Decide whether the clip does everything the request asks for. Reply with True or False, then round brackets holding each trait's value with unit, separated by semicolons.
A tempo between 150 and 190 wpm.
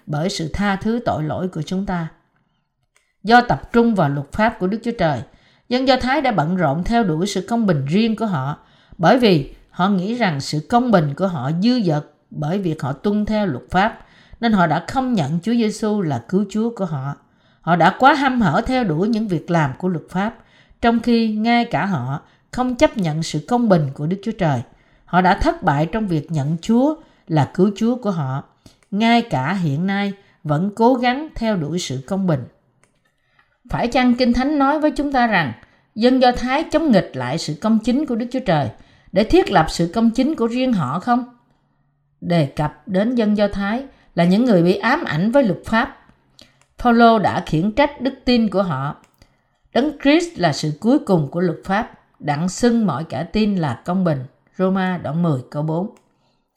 False (205 wpm)